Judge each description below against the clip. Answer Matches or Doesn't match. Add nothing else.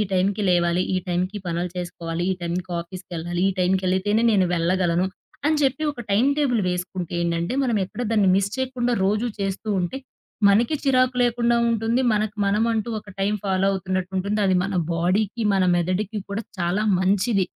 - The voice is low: Doesn't match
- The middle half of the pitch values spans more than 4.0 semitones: Doesn't match